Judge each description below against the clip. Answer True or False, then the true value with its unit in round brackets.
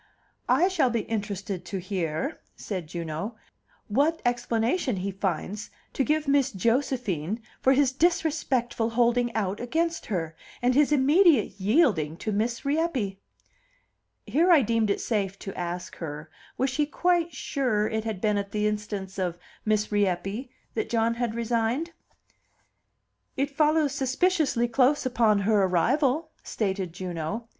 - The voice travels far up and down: True (5.9 semitones)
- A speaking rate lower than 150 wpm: True (140 wpm)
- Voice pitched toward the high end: True (230 Hz)